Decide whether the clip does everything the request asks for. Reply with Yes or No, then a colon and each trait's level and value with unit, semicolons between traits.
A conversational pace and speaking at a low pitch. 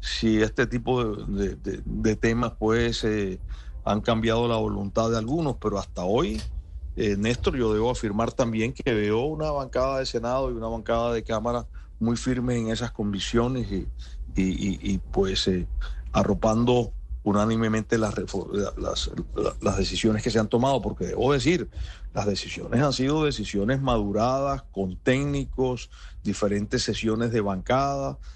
Yes: average, 155 wpm; low, 110 Hz